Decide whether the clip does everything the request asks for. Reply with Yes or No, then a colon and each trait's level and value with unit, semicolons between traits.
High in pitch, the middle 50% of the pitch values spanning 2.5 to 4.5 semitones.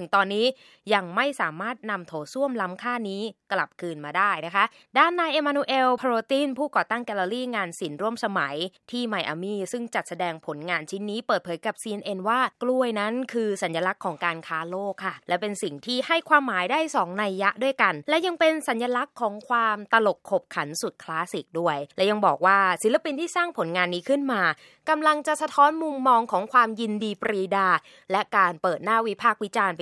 No: high, 215 Hz; average, 5.3 semitones